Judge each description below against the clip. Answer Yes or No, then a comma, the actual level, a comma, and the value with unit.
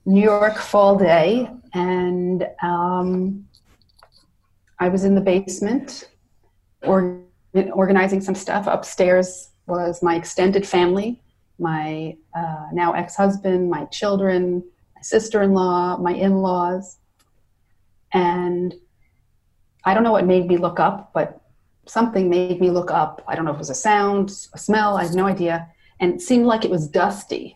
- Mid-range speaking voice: Yes, medium, 180 Hz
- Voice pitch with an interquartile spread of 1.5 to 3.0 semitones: Yes, narrow, 2.4 semitones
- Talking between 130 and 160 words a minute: Yes, average, 150 wpm